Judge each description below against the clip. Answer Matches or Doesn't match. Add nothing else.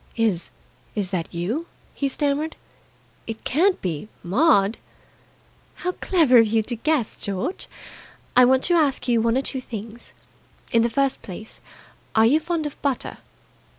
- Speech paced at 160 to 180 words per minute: Doesn't match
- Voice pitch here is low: Doesn't match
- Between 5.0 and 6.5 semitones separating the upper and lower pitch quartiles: Matches